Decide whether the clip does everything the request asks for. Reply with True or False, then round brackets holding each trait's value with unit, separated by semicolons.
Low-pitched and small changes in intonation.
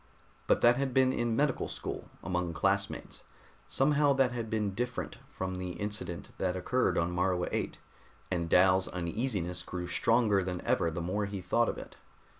False (95 Hz; 5.1 semitones)